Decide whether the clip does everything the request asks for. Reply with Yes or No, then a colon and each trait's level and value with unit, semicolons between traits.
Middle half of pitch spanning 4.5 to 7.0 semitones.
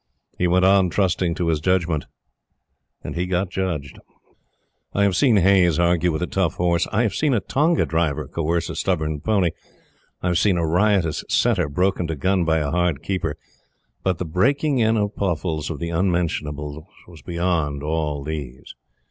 No: average, 3.3 semitones